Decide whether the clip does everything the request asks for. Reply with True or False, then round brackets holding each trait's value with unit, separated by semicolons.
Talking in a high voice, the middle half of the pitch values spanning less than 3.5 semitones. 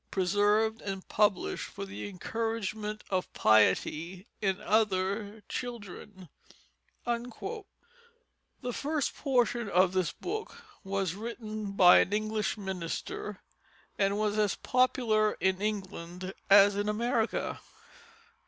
True (210 Hz; 2.6 semitones)